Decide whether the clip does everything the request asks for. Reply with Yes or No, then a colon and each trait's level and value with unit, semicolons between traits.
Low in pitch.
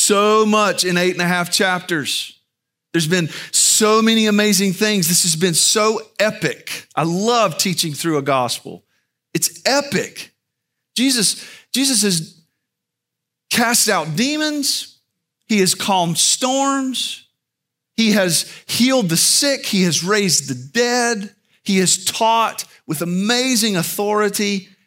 No: high, 200 Hz